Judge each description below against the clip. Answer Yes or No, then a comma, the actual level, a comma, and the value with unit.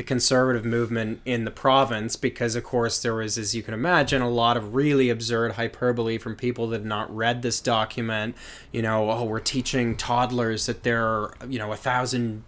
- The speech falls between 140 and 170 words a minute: No, average, 200 wpm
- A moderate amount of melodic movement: No, narrow, 1.8 semitones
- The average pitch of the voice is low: Yes, low, 120 Hz